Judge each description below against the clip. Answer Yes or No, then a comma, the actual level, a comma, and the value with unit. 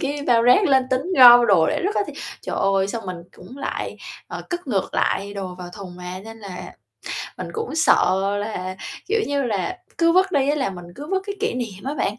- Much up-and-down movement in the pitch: Yes, wide, 7.1 semitones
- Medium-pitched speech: No, high, 240 Hz